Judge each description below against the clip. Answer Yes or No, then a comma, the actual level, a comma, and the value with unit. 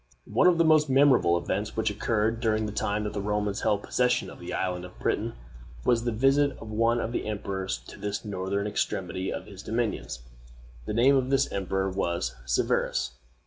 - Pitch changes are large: No, average, 3.7 semitones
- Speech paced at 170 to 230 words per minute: Yes, average, 190 wpm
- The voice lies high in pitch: No, low, 105 Hz